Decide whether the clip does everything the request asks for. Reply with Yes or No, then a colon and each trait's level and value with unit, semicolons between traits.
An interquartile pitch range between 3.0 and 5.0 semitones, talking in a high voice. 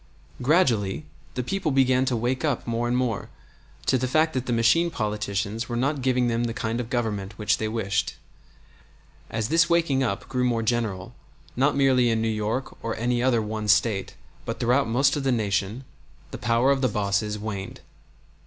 No: average, 3.3 semitones; low, 120 Hz